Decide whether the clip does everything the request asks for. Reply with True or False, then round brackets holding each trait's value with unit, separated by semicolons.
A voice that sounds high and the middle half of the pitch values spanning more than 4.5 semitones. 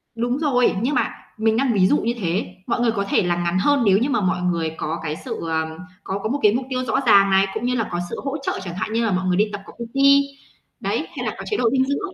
True (215 Hz; 5.3 semitones)